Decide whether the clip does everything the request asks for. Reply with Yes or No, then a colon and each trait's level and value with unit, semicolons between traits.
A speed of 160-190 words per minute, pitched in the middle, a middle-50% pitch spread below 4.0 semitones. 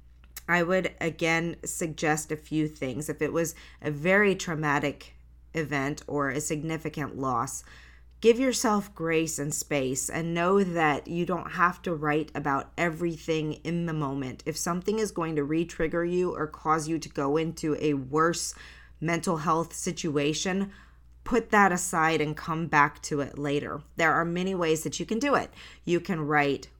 Yes: average, 170 wpm; medium, 160 Hz; average, 2.8 semitones